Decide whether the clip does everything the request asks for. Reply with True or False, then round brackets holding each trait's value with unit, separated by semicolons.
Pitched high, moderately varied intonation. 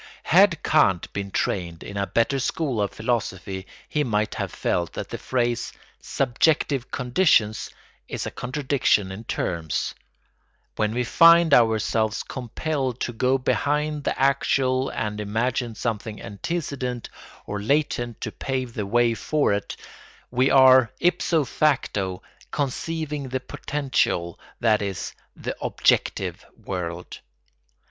False (120 Hz; 4.9 semitones)